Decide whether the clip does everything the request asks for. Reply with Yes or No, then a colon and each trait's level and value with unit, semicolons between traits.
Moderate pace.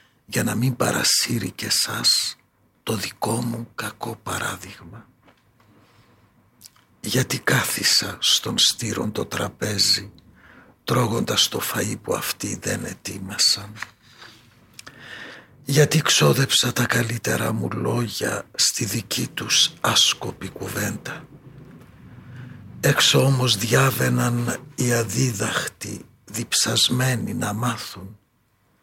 No: slow, 90 wpm